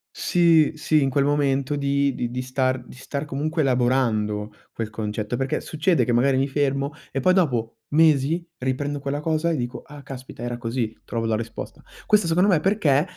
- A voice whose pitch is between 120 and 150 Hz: Yes, low, 135 Hz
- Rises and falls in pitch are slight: No, average, 3.7 semitones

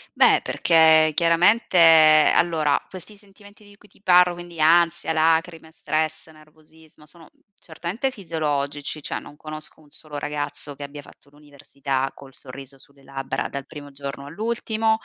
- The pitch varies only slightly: No, average, 3.2 semitones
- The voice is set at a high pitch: No, medium, 155 Hz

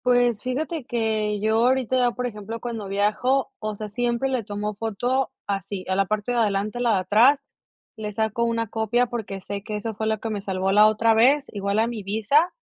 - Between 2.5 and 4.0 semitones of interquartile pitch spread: Yes, average, 2.8 semitones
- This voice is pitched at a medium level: No, high, 220 Hz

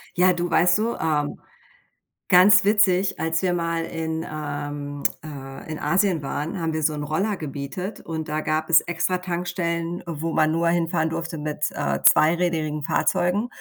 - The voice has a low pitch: No, medium, 165 Hz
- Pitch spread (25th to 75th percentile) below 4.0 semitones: Yes, narrow, 2.5 semitones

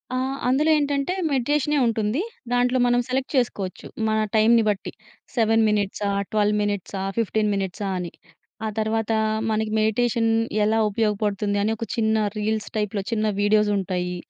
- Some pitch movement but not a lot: No, narrow, 2.3 semitones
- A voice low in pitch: No, high, 220 Hz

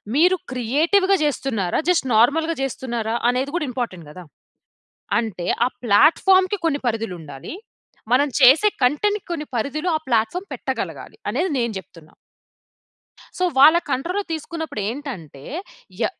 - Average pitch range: No, wide, 6.5 semitones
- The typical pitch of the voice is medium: No, very high, 270 Hz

